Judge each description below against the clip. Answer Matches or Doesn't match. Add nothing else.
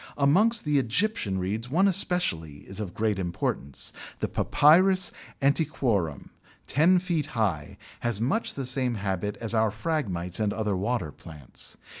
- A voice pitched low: Matches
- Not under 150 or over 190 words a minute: Doesn't match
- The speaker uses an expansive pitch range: Matches